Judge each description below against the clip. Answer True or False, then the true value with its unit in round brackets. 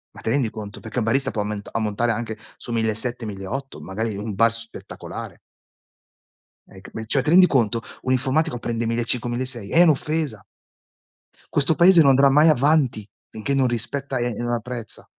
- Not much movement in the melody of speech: False (3.7 semitones)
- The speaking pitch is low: True (120 Hz)